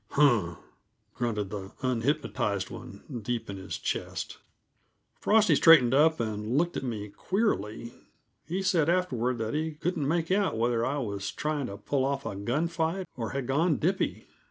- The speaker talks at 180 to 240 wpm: No, average, 160 wpm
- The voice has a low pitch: Yes, low, 130 Hz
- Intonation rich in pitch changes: Yes, wide, 6.3 semitones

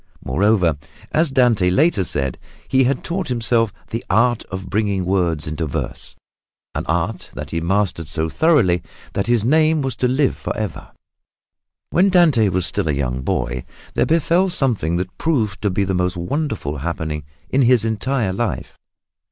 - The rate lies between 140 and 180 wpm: Yes, average, 160 wpm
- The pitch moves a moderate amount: No, wide, 7.2 semitones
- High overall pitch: No, low, 105 Hz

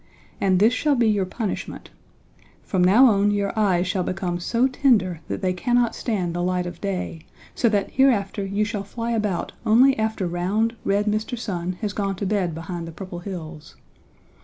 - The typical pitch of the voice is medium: No, high, 200 Hz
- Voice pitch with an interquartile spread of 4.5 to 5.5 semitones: No, average, 3.5 semitones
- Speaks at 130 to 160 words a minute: No, average, 185 wpm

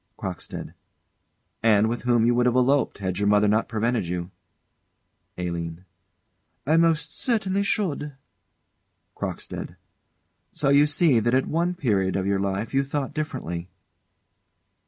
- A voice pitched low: Yes, low, 120 Hz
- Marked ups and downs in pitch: Yes, wide, 6.8 semitones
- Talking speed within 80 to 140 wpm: Yes, slow, 135 wpm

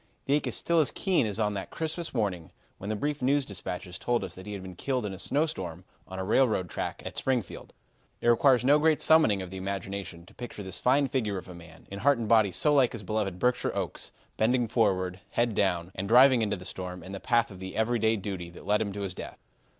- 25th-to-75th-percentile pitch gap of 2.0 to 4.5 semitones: No, average, 5.1 semitones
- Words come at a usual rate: No, fast, 240 wpm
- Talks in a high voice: No, low, 105 Hz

